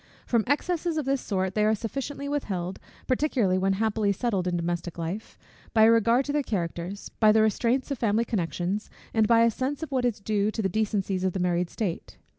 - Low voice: No, high, 215 Hz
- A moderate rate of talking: No, fast, 210 wpm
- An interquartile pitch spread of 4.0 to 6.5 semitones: Yes, average, 4.6 semitones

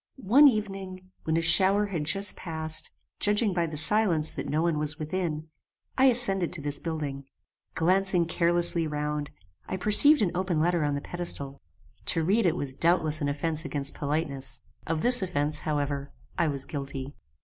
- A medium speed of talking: Yes, average, 170 wpm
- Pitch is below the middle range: No, medium, 165 Hz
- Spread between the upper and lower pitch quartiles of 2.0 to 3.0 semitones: No, average, 4.0 semitones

